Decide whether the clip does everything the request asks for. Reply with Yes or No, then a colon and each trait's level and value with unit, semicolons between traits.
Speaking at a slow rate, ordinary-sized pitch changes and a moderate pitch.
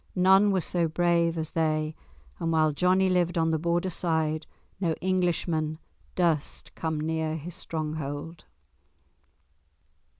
No: slow, 125 wpm; narrow, 2.0 semitones; medium, 165 Hz